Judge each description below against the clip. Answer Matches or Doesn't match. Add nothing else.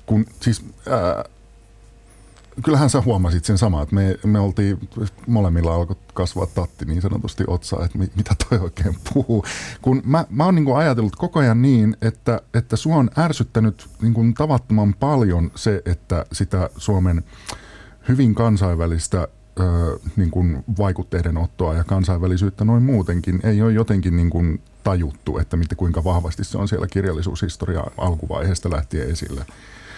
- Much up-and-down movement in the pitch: Doesn't match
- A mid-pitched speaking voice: Doesn't match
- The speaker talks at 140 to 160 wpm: Matches